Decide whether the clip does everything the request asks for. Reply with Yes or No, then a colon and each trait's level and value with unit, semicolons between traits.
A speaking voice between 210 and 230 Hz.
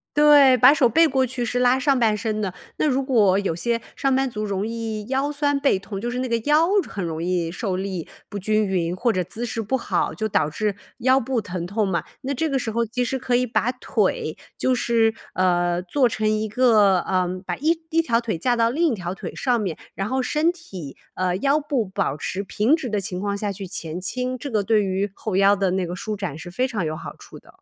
Yes: high, 220 Hz